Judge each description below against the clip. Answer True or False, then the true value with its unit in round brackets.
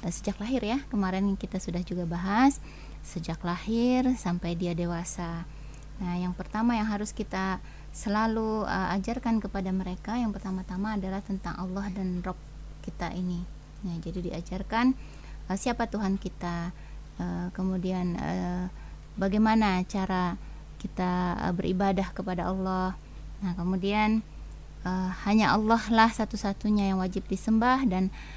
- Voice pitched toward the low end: False (190 Hz)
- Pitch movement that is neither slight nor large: True (3.1 semitones)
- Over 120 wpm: True (130 wpm)